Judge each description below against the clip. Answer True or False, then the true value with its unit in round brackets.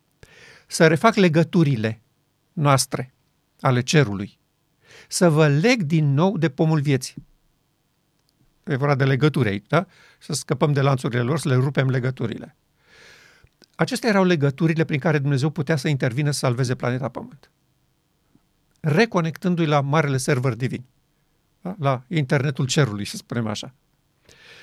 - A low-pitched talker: False (150 Hz)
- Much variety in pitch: False (3.1 semitones)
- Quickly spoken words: False (130 wpm)